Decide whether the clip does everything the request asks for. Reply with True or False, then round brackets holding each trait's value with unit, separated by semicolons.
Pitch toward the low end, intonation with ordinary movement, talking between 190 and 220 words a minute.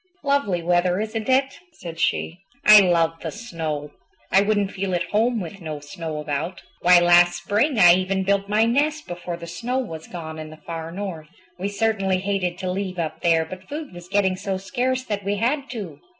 False (185 Hz; 3.7 semitones; 195 wpm)